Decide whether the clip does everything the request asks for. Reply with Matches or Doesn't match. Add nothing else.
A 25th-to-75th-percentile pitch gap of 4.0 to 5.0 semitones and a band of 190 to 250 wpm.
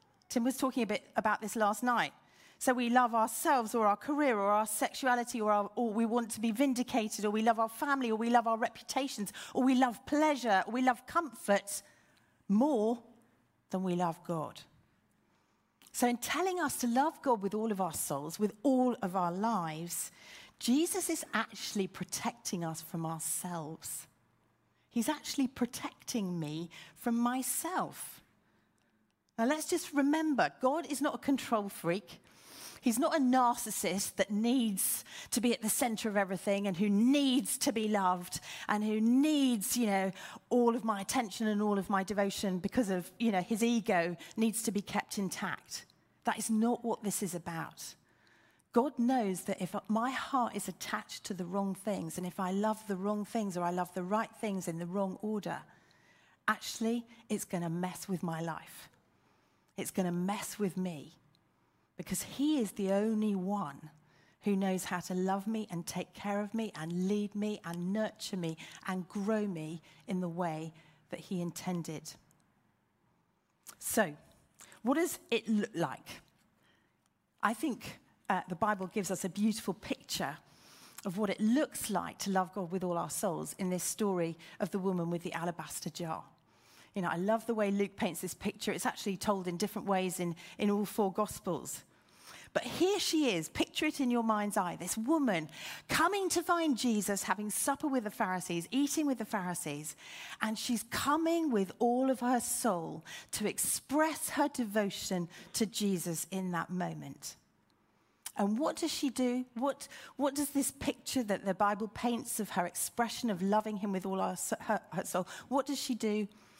Doesn't match